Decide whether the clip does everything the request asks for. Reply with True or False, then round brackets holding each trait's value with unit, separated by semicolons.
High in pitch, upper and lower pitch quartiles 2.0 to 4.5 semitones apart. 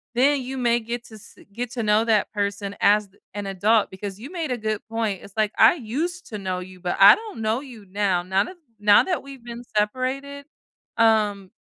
True (220 Hz; 3.8 semitones)